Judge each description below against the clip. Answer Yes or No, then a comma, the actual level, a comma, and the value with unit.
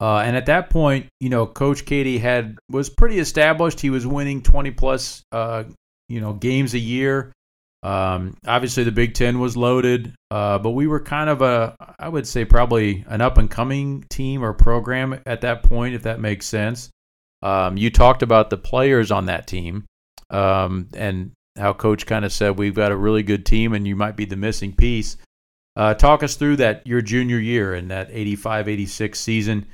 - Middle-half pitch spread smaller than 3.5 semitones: No, average, 4.0 semitones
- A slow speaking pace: No, average, 200 wpm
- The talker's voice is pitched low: Yes, low, 115 Hz